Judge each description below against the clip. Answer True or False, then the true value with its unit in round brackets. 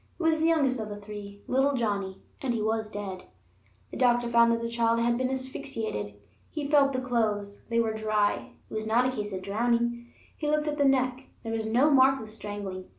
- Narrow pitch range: False (3.6 semitones)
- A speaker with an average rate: False (215 wpm)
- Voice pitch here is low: False (235 Hz)